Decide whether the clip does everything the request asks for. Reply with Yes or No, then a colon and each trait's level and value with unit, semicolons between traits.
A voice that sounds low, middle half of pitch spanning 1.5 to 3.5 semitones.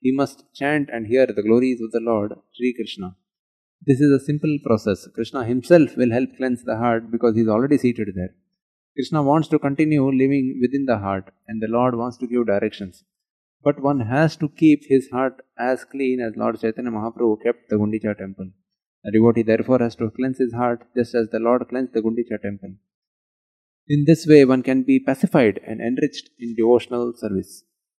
Yes: low, 120 Hz; average, 3.2 semitones